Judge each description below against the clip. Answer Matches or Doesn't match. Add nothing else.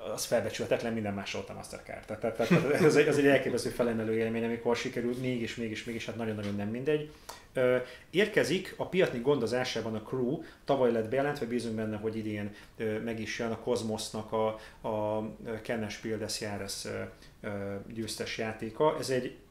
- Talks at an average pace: Doesn't match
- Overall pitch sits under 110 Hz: Doesn't match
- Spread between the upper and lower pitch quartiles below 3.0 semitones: Matches